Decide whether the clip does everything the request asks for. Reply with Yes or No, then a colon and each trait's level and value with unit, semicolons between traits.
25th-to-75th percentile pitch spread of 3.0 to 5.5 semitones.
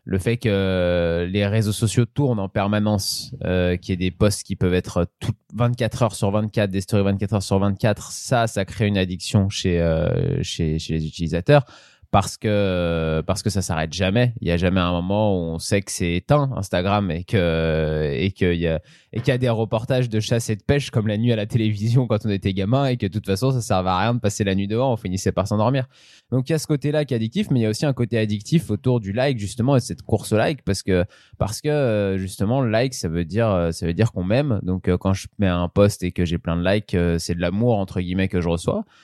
Yes: average, 4.2 semitones